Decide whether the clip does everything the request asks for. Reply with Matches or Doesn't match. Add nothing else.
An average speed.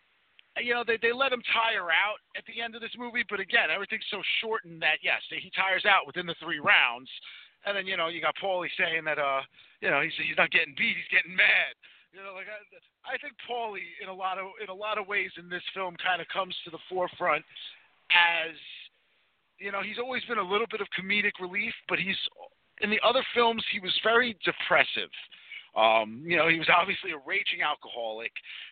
Doesn't match